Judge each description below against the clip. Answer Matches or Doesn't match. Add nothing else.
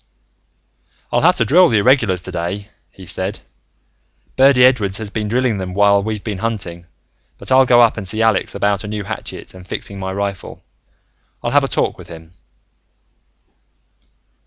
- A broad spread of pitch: Doesn't match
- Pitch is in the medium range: Doesn't match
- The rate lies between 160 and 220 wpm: Matches